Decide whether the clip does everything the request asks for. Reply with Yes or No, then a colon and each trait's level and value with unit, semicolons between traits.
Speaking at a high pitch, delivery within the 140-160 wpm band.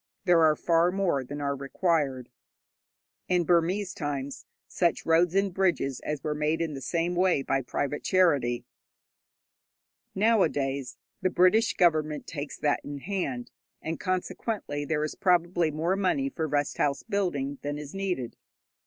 No: medium, 160 Hz; average, 155 wpm